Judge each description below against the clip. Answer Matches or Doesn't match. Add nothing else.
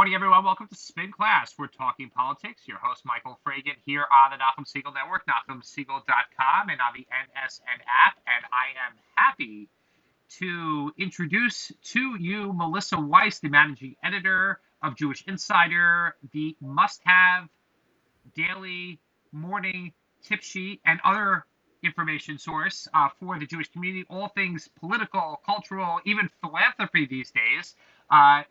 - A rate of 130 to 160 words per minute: Matches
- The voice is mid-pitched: Matches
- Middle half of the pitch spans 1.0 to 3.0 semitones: Doesn't match